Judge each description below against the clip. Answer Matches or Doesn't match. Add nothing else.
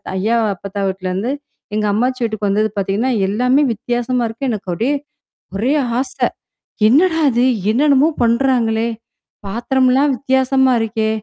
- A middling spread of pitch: Matches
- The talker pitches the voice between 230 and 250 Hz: Matches